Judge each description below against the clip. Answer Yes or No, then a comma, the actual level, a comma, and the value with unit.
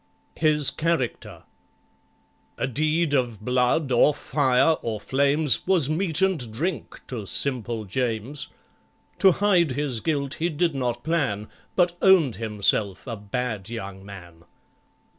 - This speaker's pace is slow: Yes, slow, 125 wpm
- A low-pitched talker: Yes, low, 130 Hz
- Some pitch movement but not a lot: No, wide, 6.1 semitones